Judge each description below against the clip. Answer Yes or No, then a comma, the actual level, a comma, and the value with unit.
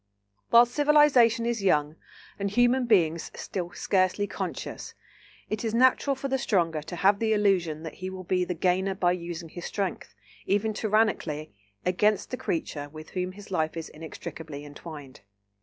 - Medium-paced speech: Yes, average, 160 wpm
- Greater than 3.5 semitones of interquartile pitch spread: Yes, average, 5.1 semitones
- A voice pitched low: No, medium, 185 Hz